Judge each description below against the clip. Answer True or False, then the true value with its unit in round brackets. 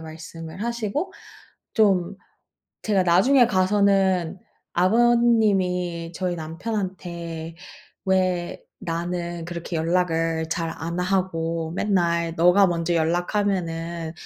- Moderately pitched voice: True (175 Hz)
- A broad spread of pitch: False (2.6 semitones)